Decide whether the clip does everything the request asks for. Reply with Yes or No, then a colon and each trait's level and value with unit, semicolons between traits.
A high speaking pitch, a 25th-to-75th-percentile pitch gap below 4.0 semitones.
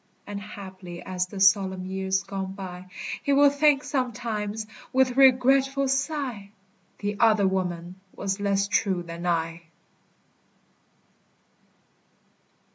No: high, 200 Hz; average, 5.2 semitones